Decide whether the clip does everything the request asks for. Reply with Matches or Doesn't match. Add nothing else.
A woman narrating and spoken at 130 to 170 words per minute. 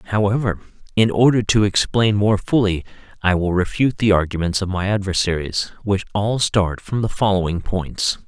Doesn't match